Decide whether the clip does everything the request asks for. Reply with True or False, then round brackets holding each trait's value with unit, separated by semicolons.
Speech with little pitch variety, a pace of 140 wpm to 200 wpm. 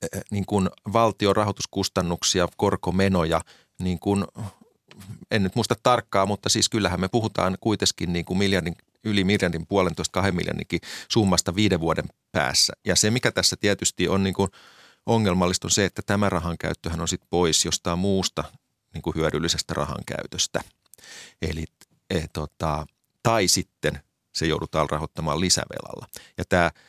False (3.1 semitones; 145 wpm)